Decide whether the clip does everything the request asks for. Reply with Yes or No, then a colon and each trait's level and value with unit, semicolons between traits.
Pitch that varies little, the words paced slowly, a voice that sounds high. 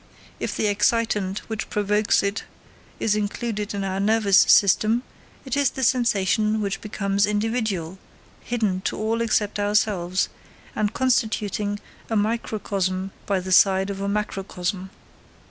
Yes: narrow, 2.0 semitones; slow, 130 wpm; high, 205 Hz